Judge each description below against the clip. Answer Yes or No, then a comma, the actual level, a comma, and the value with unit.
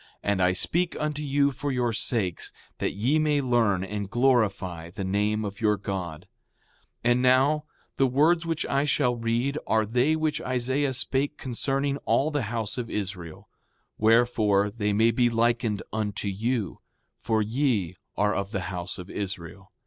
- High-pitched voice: No, low, 115 Hz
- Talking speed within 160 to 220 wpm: Yes, average, 165 wpm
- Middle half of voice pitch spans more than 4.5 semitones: Yes, average, 5.1 semitones